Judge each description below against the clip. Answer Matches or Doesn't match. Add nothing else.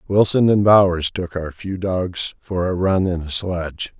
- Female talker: Doesn't match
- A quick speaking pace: Doesn't match